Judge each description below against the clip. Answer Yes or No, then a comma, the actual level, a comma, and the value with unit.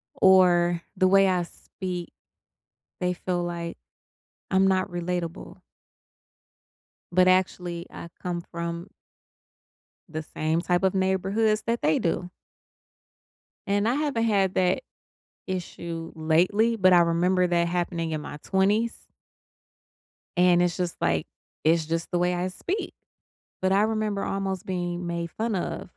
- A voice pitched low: No, medium, 180 Hz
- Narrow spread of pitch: Yes, narrow, 2.0 semitones